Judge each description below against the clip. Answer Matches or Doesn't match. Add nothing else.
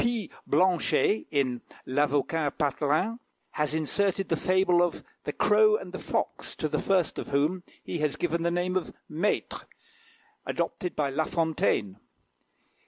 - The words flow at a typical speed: Matches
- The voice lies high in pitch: Doesn't match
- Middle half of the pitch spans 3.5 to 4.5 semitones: Matches